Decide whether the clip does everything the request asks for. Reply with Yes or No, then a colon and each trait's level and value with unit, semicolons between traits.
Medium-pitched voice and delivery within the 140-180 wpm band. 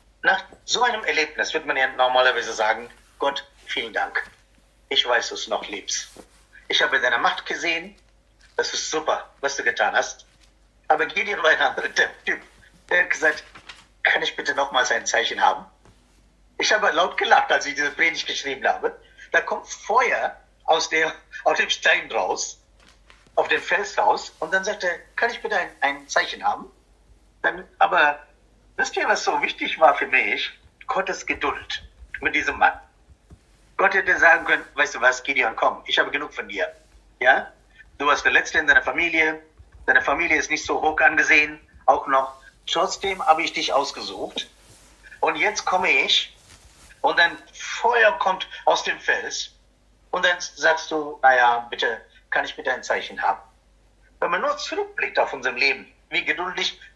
Yes: medium, 170 Hz; average, 175 wpm